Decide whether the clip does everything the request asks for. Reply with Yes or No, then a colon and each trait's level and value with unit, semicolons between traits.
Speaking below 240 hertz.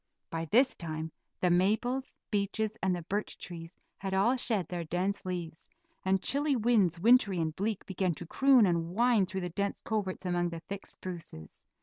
Yes: high, 190 Hz